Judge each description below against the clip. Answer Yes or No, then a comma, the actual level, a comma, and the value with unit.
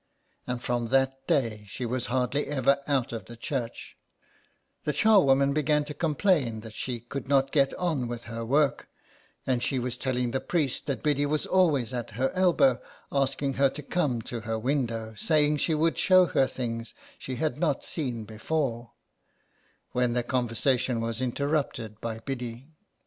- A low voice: Yes, low, 130 Hz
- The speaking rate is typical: Yes, average, 165 wpm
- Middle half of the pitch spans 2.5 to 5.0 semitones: Yes, average, 3.6 semitones